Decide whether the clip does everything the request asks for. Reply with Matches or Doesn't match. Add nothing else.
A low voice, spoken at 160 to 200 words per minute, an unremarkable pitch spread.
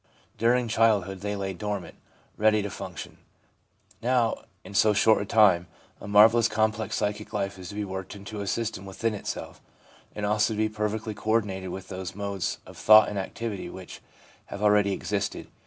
Doesn't match